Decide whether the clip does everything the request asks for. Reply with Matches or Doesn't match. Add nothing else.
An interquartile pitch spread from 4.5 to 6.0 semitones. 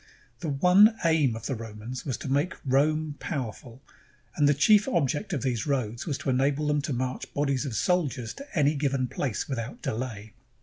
Doesn't match